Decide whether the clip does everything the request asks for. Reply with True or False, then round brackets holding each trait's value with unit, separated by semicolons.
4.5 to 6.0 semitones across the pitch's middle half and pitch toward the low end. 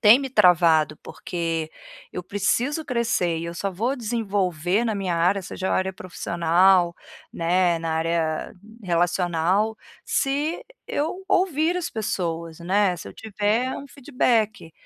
False (5.5 semitones; 190 Hz)